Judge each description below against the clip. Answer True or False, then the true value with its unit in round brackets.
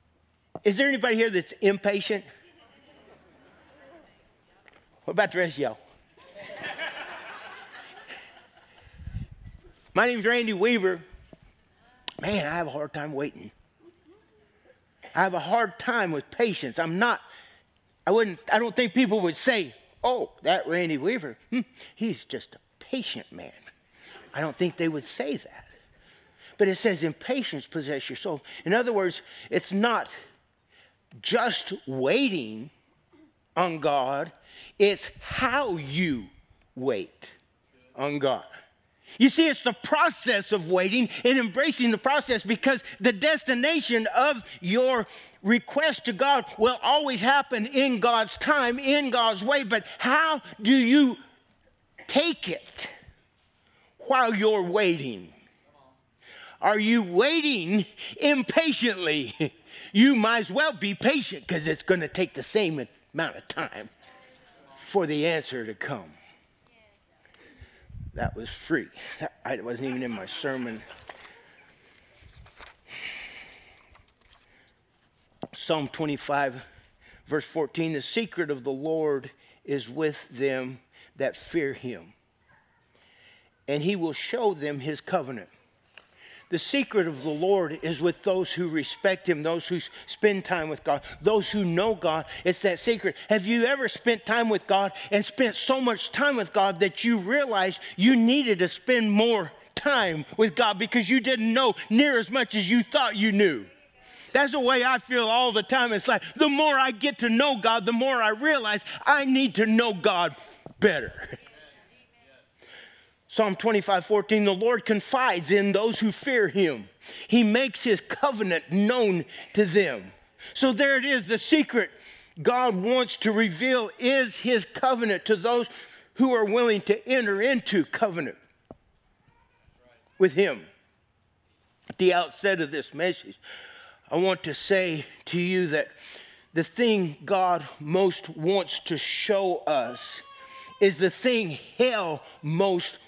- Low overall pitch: False (210 Hz)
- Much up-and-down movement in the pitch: True (6.5 semitones)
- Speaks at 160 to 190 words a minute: False (140 wpm)